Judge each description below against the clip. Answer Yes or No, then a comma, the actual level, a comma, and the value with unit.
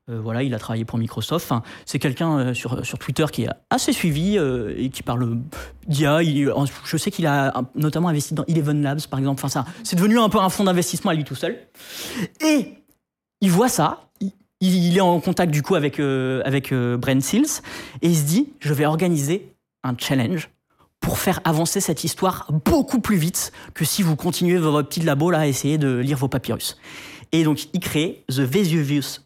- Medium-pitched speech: Yes, medium, 155 Hz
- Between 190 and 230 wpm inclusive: Yes, average, 210 wpm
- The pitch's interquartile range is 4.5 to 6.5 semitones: Yes, average, 4.9 semitones